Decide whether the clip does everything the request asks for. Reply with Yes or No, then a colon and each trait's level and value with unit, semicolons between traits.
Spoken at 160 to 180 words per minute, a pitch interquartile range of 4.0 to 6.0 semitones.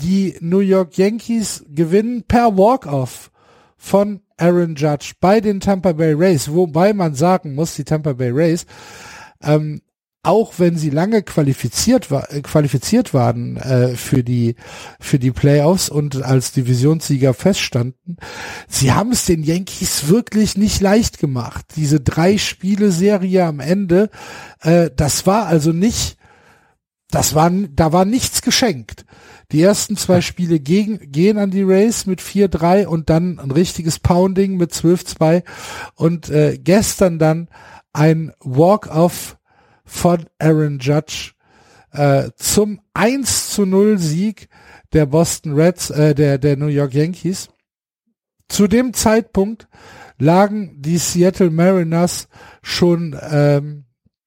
No: average, 130 wpm; average, 4.7 semitones